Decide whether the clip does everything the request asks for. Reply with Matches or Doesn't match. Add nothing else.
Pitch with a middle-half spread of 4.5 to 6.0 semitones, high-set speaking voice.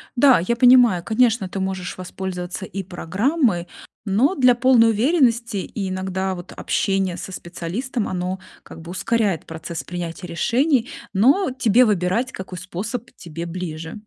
Matches